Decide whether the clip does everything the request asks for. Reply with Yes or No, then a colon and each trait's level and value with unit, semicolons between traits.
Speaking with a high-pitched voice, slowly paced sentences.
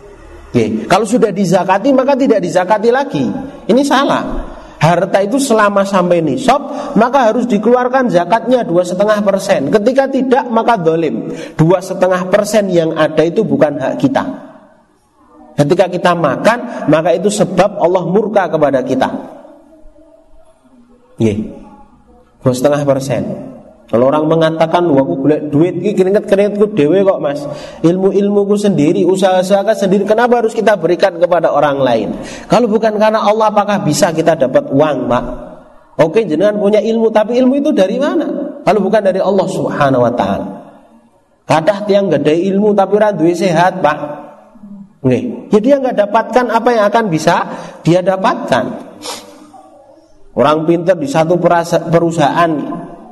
No: high, 205 Hz; fast, 140 wpm